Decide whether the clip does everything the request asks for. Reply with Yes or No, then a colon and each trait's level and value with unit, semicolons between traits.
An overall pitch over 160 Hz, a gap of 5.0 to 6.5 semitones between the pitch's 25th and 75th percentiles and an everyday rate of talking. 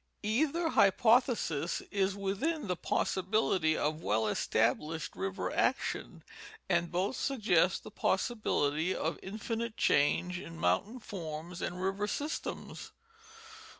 No: high, 190 Hz; wide, 5.6 semitones; slow, 110 wpm